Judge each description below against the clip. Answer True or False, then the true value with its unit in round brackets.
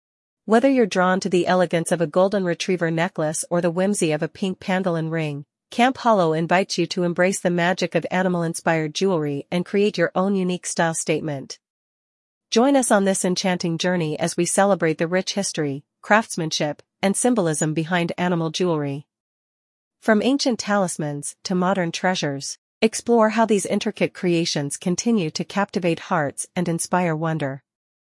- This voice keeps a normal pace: True (160 wpm)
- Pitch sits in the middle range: True (180 Hz)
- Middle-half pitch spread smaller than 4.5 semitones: True (3.1 semitones)